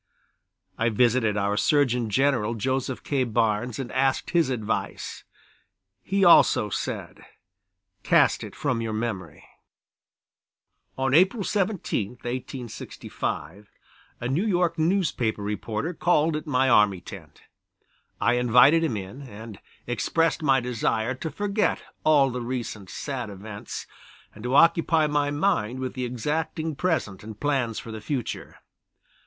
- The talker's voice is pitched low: Yes, low, 125 Hz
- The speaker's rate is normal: No, slow, 130 wpm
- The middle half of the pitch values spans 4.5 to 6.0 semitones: Yes, wide, 5.4 semitones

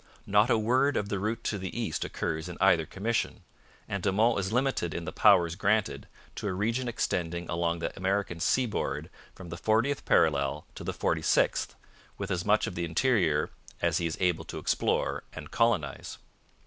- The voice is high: No, very low, 95 Hz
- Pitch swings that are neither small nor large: Yes, average, 4.7 semitones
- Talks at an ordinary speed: Yes, average, 185 wpm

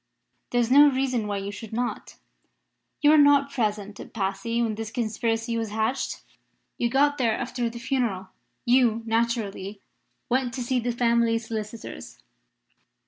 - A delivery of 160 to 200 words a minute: No, average, 150 wpm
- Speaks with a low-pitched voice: No, high, 235 Hz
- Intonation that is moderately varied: No, narrow, 2.3 semitones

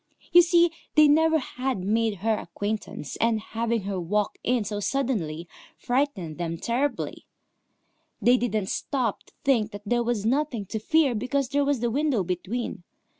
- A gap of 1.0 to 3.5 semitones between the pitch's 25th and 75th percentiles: No, average, 5.0 semitones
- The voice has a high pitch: Yes, high, 235 Hz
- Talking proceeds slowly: No, average, 160 wpm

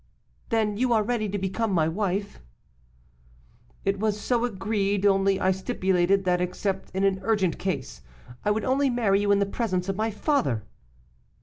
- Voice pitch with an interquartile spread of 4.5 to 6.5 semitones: No, narrow, 2.5 semitones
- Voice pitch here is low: No, high, 200 Hz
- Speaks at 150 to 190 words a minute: Yes, average, 170 wpm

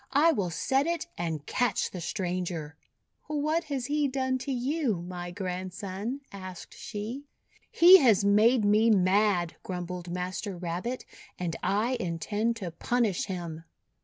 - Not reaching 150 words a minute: Yes, slow, 135 wpm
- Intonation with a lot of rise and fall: Yes, wide, 6.3 semitones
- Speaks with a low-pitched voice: No, high, 205 Hz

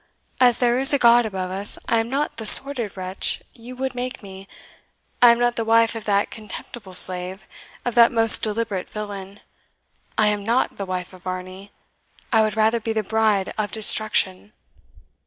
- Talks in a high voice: Yes, high, 215 Hz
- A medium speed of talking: Yes, average, 180 wpm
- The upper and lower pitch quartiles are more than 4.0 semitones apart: No, average, 3.2 semitones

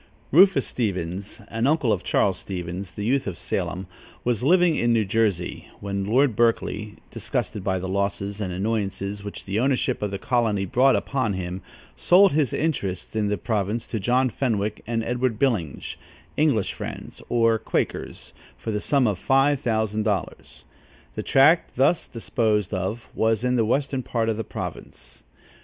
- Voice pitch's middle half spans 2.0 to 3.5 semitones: No, average, 4.2 semitones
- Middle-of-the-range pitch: No, low, 110 Hz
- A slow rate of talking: No, average, 165 wpm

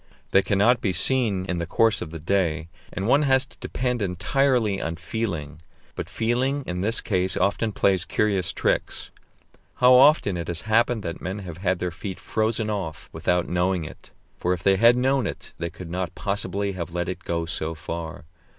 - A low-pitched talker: Yes, very low, 95 Hz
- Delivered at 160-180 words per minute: No, average, 190 wpm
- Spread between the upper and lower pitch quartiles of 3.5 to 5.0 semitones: Yes, average, 4.6 semitones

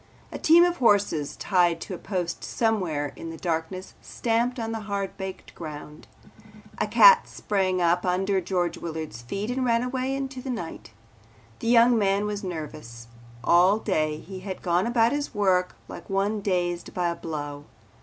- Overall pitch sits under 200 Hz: Yes, high, 190 Hz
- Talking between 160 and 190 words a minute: Yes, average, 170 wpm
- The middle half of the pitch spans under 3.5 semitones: No, average, 5.0 semitones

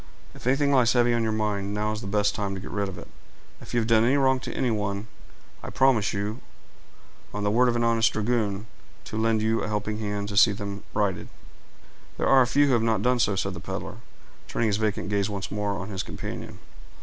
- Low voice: Yes, low, 105 Hz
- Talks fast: Yes, fast, 225 wpm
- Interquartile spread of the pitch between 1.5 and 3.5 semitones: Yes, narrow, 2.5 semitones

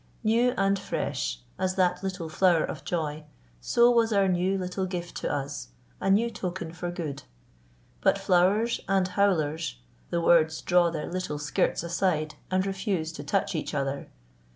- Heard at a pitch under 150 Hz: No, medium, 180 Hz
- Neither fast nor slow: Yes, average, 160 wpm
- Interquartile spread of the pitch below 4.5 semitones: Yes, average, 3.5 semitones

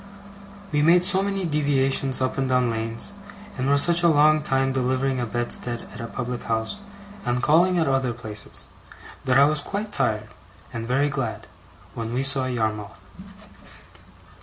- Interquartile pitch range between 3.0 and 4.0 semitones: Yes, average, 3.7 semitones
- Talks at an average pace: Yes, average, 160 wpm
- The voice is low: Yes, low, 130 Hz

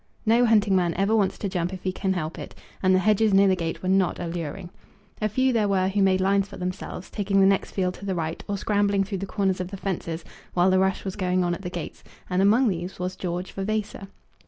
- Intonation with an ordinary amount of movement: No, narrow, 1.7 semitones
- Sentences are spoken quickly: Yes, fast, 250 wpm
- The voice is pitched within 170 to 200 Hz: Yes, high, 190 Hz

